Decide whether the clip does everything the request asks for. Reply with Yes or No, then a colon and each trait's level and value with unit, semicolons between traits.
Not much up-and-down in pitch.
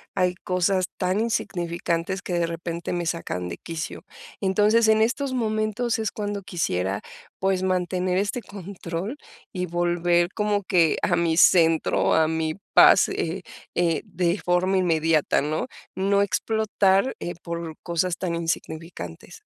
No: average, 3.1 semitones